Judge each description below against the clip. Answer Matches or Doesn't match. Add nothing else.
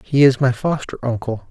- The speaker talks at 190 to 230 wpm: Matches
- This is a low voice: Matches